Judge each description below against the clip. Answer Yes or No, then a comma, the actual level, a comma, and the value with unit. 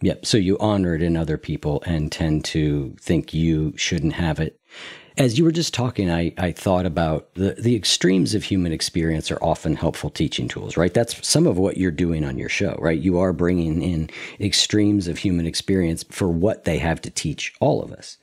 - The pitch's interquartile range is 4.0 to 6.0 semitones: No, average, 3.4 semitones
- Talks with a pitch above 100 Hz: No, very low, 85 Hz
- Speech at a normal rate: No, fast, 210 wpm